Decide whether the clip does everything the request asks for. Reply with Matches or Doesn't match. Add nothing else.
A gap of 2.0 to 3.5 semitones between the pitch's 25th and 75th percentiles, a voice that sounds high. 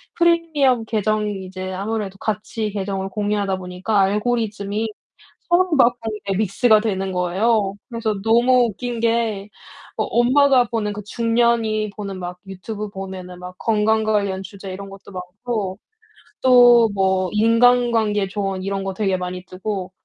Matches